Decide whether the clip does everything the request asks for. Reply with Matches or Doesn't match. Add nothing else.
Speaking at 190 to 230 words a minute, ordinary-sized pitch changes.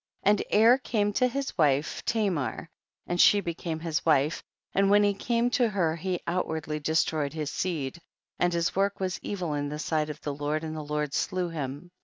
Matches